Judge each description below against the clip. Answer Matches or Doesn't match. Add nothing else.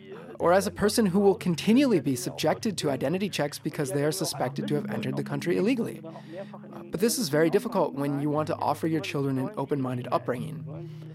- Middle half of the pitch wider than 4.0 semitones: Matches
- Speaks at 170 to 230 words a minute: Matches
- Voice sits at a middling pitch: Matches